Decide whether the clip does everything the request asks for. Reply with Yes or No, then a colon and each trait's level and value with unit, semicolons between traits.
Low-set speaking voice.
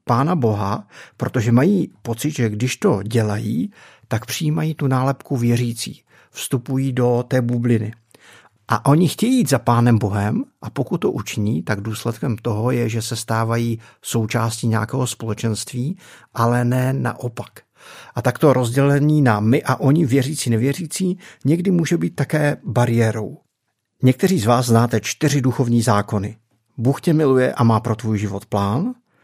Yes: low, 120 Hz